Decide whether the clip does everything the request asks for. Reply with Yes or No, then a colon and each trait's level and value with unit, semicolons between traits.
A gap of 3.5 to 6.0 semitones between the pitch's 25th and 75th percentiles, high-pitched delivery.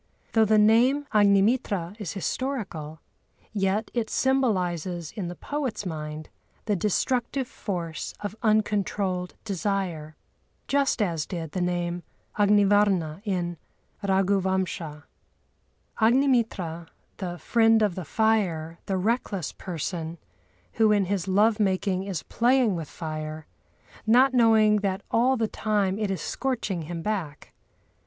Yes: average, 4.1 semitones; high, 195 Hz